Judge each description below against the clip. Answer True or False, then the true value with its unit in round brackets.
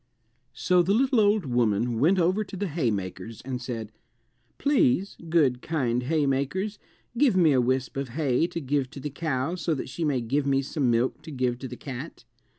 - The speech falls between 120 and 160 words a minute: False (190 wpm)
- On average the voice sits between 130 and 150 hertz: True (140 Hz)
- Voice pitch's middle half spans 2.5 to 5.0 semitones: False (5.5 semitones)